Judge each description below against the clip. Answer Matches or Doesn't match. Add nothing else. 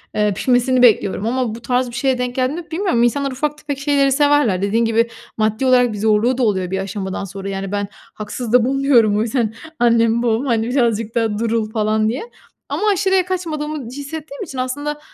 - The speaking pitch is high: Matches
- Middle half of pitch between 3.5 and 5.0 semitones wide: Matches